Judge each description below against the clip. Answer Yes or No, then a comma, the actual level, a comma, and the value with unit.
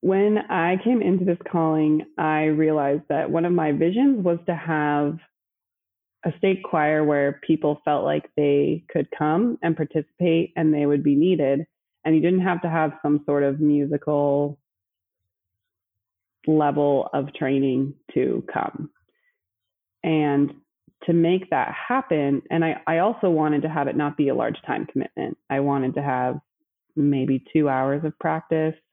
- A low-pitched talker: No, medium, 150 Hz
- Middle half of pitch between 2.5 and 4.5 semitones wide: Yes, average, 2.8 semitones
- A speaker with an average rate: Yes, average, 160 wpm